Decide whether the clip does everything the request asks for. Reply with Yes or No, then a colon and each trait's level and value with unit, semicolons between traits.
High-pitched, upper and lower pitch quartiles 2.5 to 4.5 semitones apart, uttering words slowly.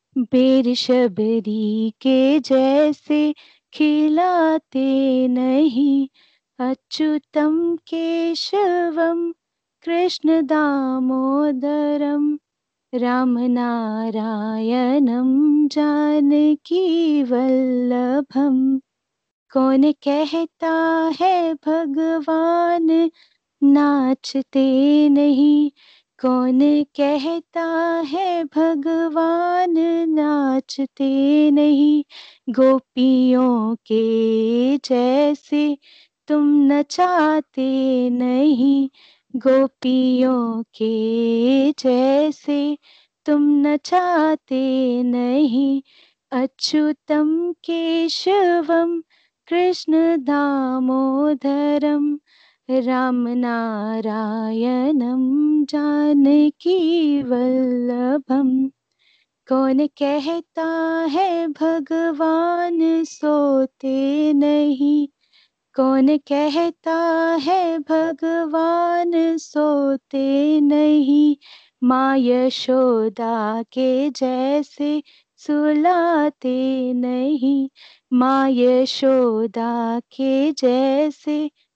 Yes: very high, 290 Hz; average, 3.5 semitones; slow, 50 wpm